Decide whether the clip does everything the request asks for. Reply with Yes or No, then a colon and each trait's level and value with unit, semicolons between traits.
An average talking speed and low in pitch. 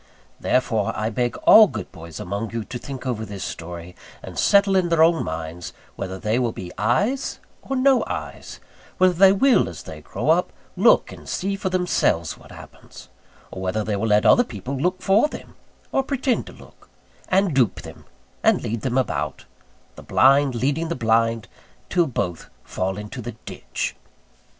Yes: average, 180 wpm; low, 125 Hz